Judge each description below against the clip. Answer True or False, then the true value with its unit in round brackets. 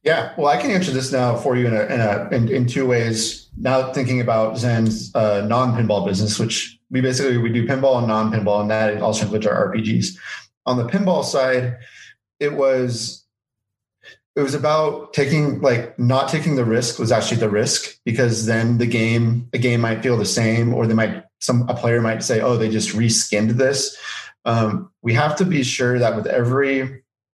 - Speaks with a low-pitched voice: True (120 Hz)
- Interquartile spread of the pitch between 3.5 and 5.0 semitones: False (2.8 semitones)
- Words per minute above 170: True (200 wpm)